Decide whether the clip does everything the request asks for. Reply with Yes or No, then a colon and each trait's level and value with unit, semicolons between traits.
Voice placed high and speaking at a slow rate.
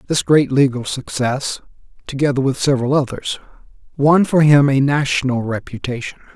No: low, 135 Hz; slow, 130 wpm